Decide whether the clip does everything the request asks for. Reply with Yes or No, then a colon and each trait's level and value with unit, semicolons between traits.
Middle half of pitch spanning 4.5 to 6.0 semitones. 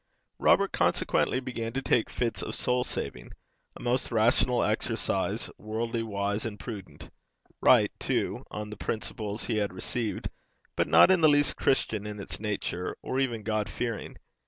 No: average, 2.8 semitones